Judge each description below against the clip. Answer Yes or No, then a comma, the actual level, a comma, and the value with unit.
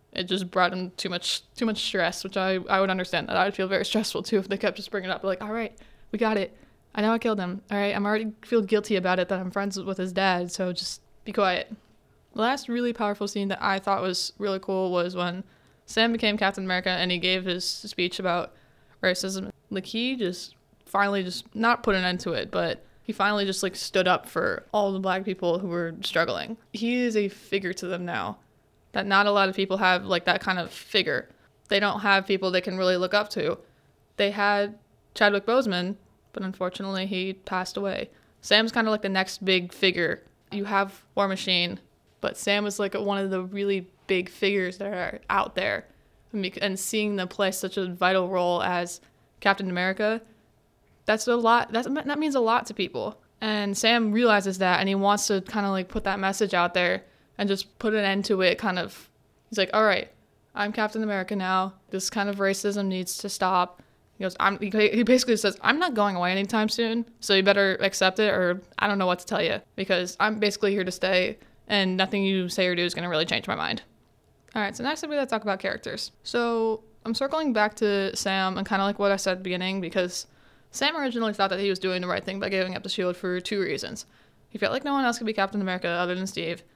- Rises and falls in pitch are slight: Yes, narrow, 2.3 semitones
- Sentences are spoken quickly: Yes, fast, 230 wpm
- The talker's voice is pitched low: No, high, 195 Hz